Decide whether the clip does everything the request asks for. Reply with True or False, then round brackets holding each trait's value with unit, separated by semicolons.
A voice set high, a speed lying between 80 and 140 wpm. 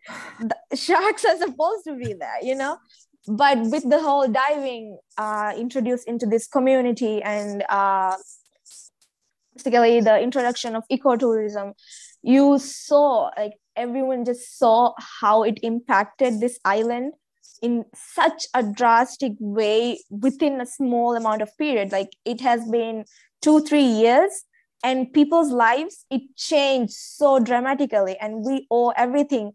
True (245 Hz; 135 wpm)